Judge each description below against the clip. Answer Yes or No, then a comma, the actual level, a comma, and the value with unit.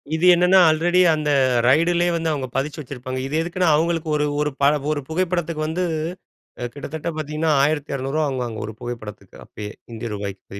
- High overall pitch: No, medium, 155 Hz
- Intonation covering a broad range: No, average, 4.3 semitones